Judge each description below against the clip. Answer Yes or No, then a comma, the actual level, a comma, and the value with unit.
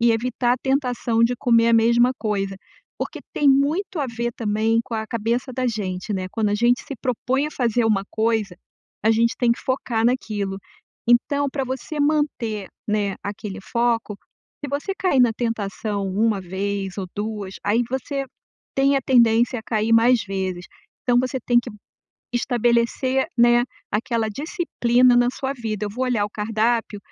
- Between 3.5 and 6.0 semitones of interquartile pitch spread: No, average, 3.1 semitones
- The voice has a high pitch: Yes, high, 235 Hz